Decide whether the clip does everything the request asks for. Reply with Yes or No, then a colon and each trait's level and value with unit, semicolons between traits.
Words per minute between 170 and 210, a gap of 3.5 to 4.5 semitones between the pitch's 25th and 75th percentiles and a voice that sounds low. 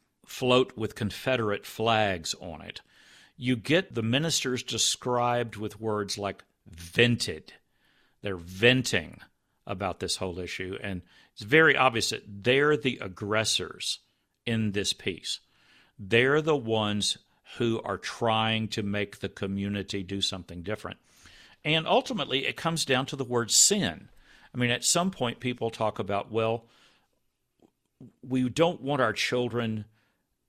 No: slow, 135 wpm; average, 3.9 semitones; low, 115 Hz